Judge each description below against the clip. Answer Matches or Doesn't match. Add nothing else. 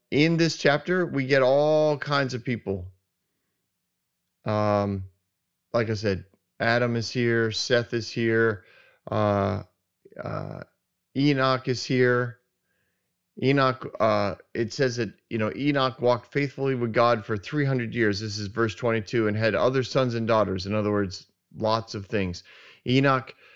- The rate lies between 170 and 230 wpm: Doesn't match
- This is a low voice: Matches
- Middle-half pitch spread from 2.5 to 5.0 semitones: Matches